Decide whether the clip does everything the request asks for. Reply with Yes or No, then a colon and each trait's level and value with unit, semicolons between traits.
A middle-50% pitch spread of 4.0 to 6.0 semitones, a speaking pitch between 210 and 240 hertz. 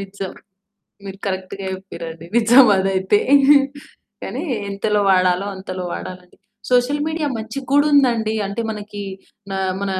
No: average, 4.3 semitones; high, 200 Hz